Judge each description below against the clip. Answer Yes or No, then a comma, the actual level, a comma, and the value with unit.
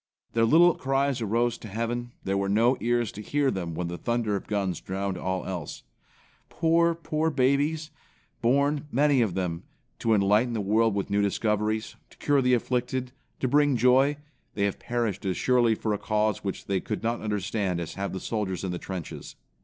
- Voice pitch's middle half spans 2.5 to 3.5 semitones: No, average, 4.6 semitones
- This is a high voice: No, low, 115 Hz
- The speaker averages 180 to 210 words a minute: Yes, average, 190 wpm